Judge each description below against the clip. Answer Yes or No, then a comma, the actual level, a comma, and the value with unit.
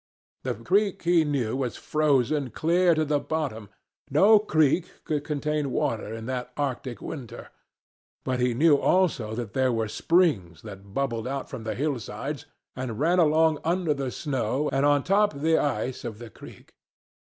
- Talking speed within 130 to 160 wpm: Yes, average, 155 wpm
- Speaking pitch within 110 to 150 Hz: Yes, medium, 140 Hz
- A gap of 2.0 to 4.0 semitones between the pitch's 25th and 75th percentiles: No, average, 4.8 semitones